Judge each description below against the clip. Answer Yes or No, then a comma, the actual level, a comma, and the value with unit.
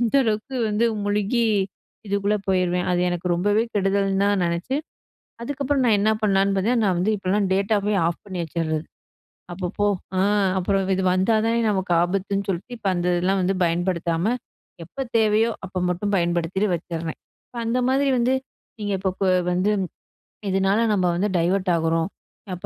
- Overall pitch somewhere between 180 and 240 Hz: Yes, high, 195 Hz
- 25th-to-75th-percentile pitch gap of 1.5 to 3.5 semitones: Yes, average, 2.9 semitones